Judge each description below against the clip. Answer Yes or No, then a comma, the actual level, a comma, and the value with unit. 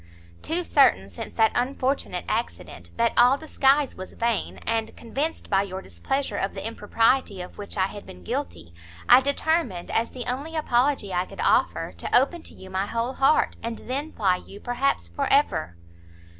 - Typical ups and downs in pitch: No, wide, 6.3 semitones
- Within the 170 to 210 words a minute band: Yes, average, 175 wpm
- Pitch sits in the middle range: No, high, 230 Hz